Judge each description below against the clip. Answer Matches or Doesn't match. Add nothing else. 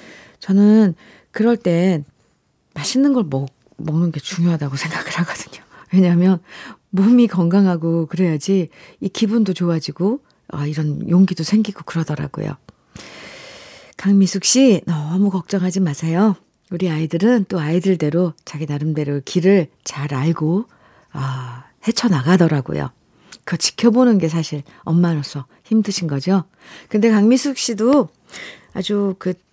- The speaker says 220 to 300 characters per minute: Matches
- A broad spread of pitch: Doesn't match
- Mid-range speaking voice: Matches